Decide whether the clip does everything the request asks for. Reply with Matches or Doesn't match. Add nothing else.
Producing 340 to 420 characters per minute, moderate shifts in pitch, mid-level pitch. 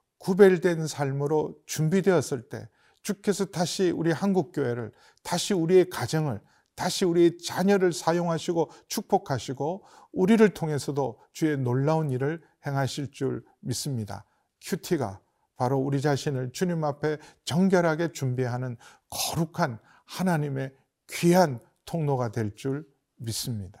Doesn't match